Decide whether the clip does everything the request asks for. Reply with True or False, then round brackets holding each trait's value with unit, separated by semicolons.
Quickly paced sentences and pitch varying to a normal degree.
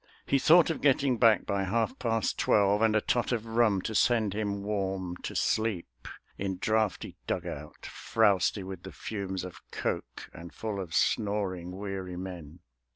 False (160 wpm; 3.1 semitones)